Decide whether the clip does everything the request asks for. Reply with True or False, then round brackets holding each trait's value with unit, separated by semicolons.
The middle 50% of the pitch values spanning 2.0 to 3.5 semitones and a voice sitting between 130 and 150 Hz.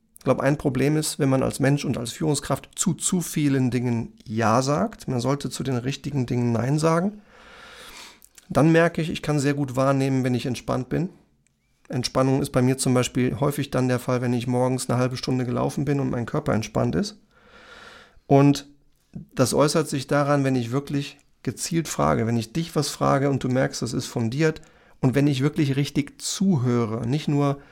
True (3.1 semitones; 140 Hz)